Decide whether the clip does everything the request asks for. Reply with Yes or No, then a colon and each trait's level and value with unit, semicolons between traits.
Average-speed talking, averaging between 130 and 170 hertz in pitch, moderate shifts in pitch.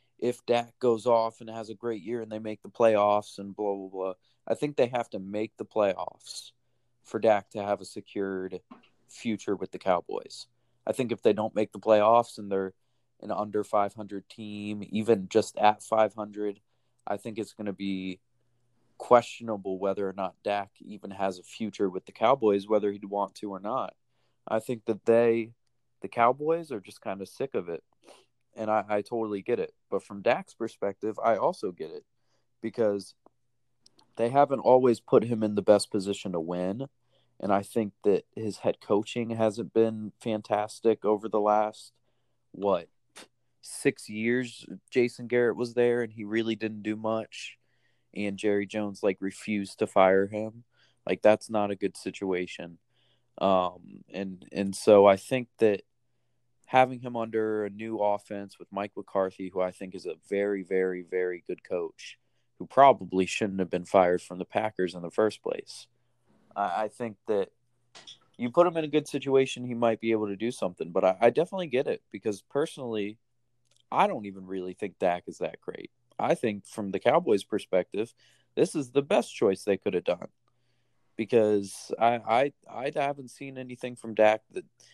No: average, 180 wpm; low, 110 Hz; average, 3.1 semitones